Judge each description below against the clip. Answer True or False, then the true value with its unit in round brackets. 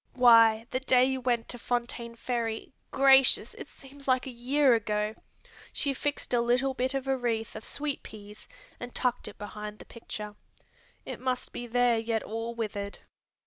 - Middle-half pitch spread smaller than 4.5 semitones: True (2.5 semitones)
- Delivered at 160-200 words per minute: True (170 wpm)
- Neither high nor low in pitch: False (240 Hz)